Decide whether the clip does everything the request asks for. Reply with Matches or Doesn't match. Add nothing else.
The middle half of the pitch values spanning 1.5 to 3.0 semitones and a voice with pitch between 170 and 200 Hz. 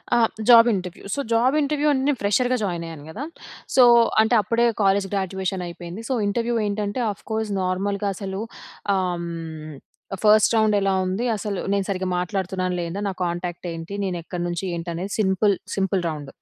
Doesn't match